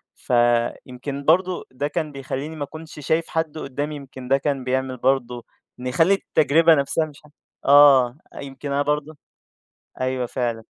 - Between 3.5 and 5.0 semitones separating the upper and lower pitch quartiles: No, average, 3.0 semitones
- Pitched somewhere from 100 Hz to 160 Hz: Yes, medium, 140 Hz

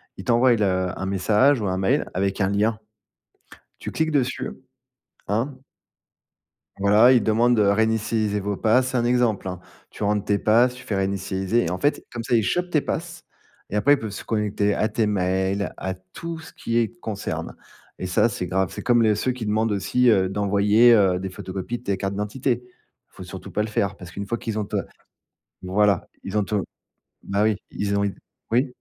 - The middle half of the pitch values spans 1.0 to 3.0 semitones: No, average, 3.4 semitones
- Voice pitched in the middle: No, low, 105 Hz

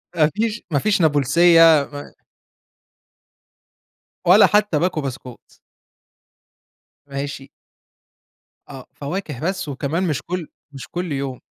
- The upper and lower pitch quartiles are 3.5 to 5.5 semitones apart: Yes, average, 4.4 semitones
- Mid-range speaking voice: Yes, medium, 155 Hz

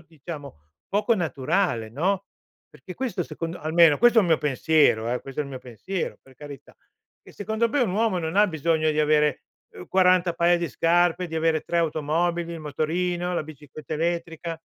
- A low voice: No, medium, 165 Hz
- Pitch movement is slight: No, average, 3.1 semitones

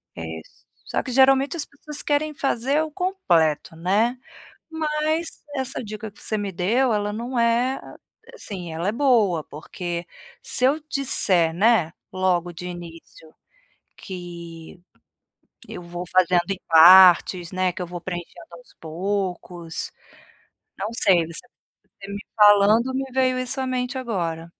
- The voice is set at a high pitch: Yes, high, 200 Hz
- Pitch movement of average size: No, wide, 6.8 semitones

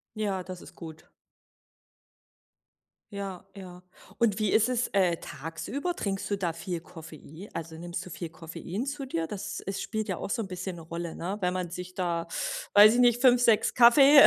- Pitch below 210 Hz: Yes, high, 190 Hz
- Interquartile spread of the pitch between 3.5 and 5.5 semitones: Yes, average, 4.1 semitones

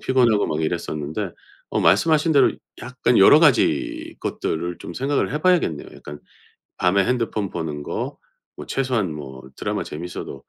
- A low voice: Yes, low, 100 Hz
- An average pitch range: No, wide, 9.0 semitones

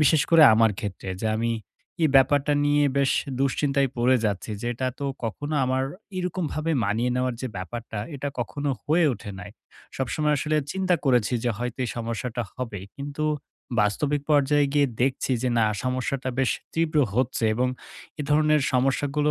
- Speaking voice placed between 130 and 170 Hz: Yes, low, 135 Hz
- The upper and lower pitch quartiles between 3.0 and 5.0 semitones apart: Yes, average, 3.5 semitones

